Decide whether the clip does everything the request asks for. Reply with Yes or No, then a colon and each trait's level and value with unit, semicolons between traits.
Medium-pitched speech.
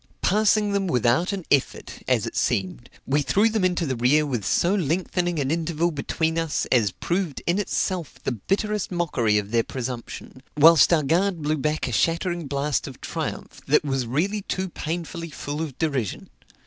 Yes: medium, 160 Hz